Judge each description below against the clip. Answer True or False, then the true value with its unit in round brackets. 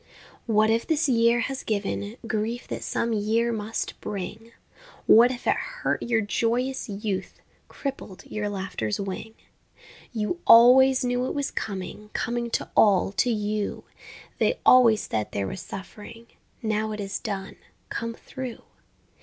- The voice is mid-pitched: False (225 Hz)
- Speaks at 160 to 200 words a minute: False (145 wpm)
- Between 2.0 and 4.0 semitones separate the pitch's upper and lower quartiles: True (2.7 semitones)